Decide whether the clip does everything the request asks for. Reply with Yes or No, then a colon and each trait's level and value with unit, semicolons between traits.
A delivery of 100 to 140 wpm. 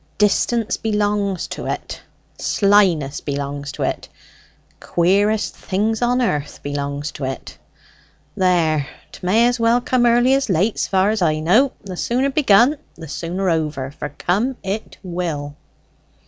Yes: slow, 135 wpm